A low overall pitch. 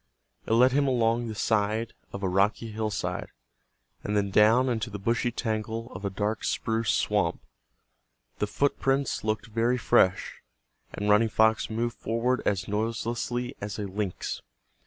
Yes: low, 110 Hz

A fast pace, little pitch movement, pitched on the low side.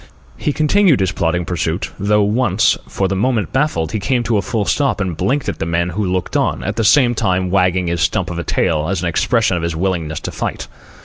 No: fast, 235 wpm; average, 4.8 semitones; very low, 95 Hz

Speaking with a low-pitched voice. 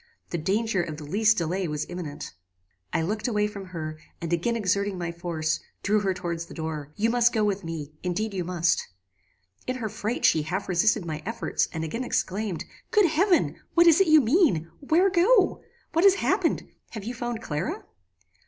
No: high, 195 Hz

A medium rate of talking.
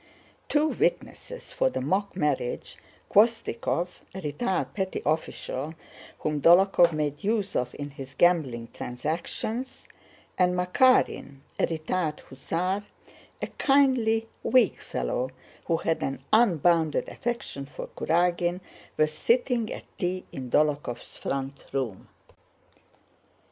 No: slow, 105 wpm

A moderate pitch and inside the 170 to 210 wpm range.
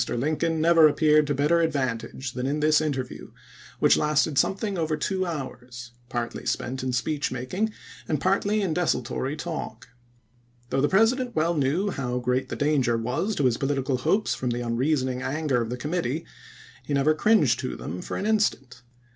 Yes: medium, 145 Hz; average, 180 wpm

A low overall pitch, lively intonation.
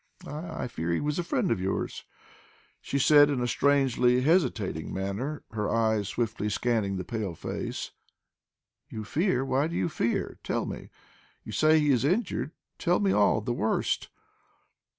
Yes: low, 125 Hz; wide, 6.1 semitones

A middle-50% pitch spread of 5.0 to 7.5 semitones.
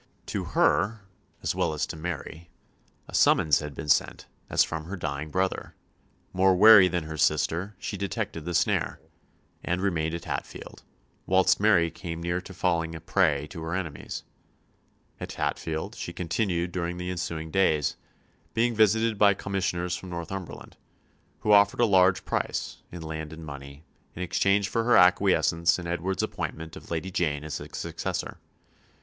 No: average, 3.1 semitones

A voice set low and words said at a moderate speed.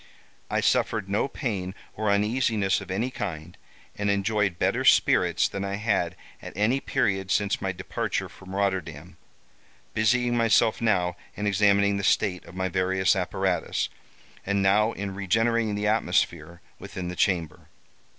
Yes: low, 100 Hz; average, 145 wpm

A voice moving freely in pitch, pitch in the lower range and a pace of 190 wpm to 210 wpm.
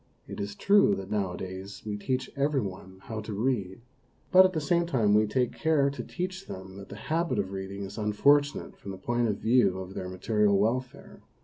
Yes: wide, 6.0 semitones; low, 105 Hz; fast, 205 wpm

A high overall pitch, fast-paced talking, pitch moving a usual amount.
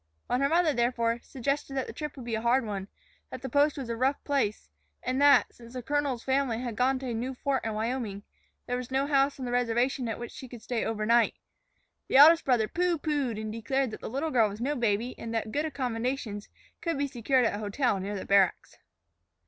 Yes: very high, 250 Hz; fast, 230 wpm; average, 3.3 semitones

